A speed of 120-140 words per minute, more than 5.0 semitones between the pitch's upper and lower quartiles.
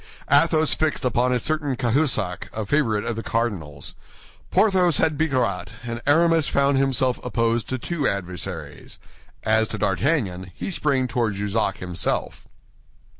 Yes: slow, 135 wpm; wide, 5.6 semitones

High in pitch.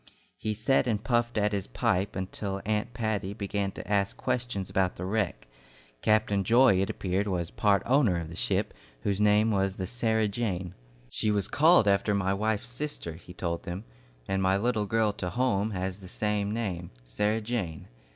No: low, 105 Hz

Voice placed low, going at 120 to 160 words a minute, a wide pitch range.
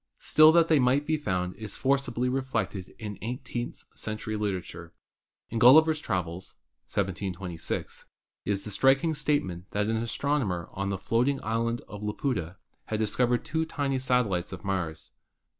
Yes: low, 110 Hz; average, 140 wpm; wide, 5.8 semitones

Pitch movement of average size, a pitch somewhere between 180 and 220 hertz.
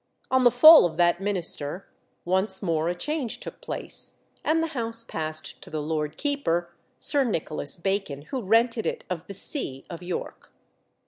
No: wide, 7.0 semitones; high, 190 Hz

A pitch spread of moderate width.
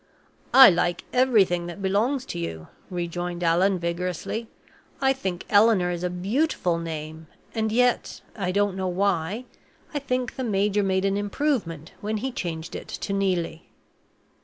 Yes: average, 4.2 semitones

